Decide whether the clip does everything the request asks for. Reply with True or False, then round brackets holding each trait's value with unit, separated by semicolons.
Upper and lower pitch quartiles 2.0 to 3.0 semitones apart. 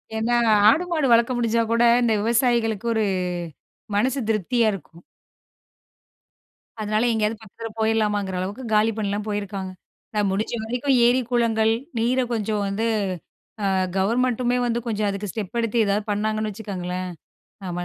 True (2.4 semitones)